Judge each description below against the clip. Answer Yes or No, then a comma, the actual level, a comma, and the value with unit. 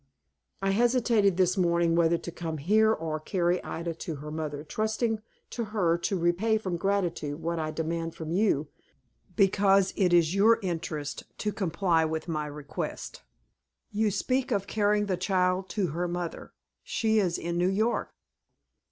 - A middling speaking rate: Yes, average, 160 wpm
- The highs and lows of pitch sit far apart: No, average, 3.8 semitones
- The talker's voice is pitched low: No, medium, 180 Hz